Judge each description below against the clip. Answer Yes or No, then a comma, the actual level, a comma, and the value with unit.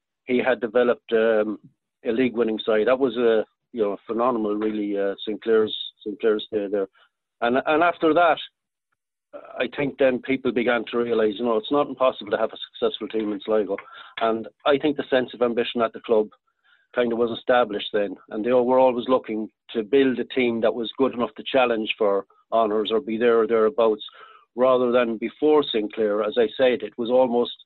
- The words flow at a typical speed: Yes, average, 195 wpm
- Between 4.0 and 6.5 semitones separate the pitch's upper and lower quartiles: No, average, 2.9 semitones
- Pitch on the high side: No, low, 120 Hz